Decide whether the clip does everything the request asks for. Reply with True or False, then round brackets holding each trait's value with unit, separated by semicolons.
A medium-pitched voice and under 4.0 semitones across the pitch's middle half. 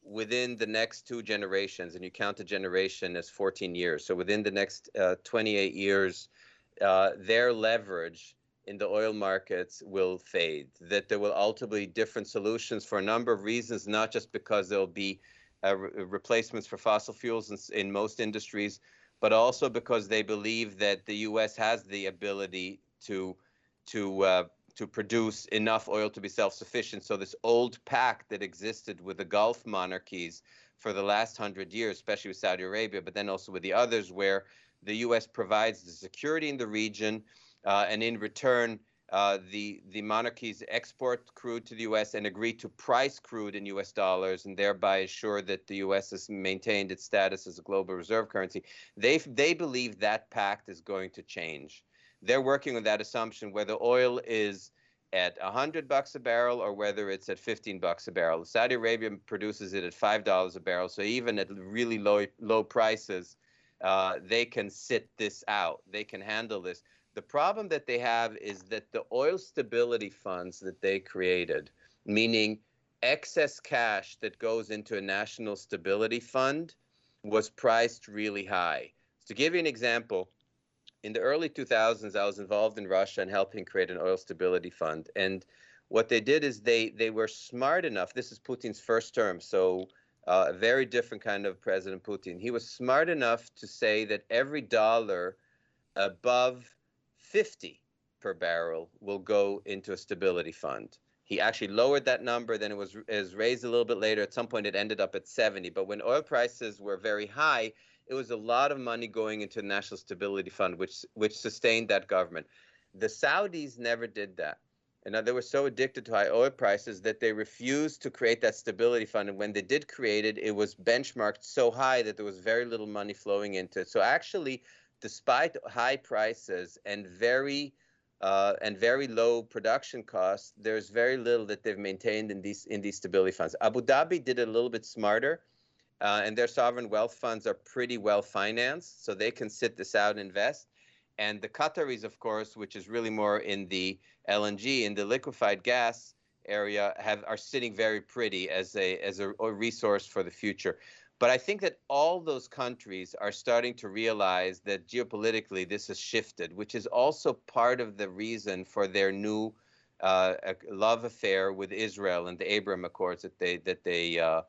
False (105 Hz; 3.1 semitones)